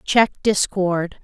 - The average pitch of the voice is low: No, high, 190 Hz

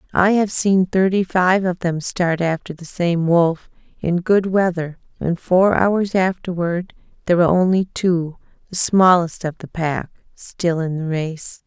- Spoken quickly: No, average, 165 wpm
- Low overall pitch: No, medium, 175 Hz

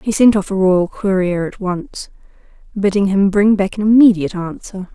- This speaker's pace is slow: No, average, 180 wpm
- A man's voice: No, female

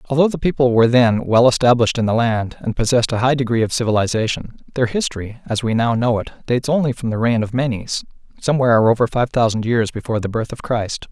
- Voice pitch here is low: Yes, low, 120 Hz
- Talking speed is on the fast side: Yes, fast, 220 wpm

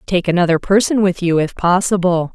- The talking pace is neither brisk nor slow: Yes, average, 180 wpm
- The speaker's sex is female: Yes, female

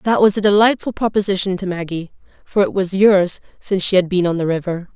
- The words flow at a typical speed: No, fast, 220 wpm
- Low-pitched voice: No, high, 190 Hz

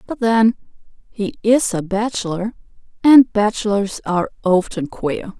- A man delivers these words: No, female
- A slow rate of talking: Yes, slow, 120 wpm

